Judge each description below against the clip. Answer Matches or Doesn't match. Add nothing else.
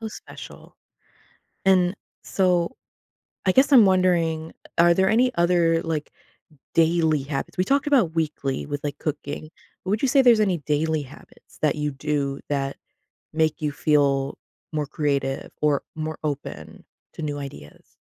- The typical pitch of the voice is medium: Matches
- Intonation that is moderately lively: Matches